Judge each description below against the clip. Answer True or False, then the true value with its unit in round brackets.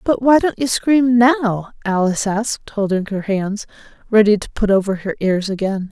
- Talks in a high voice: True (215 Hz)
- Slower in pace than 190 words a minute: True (180 wpm)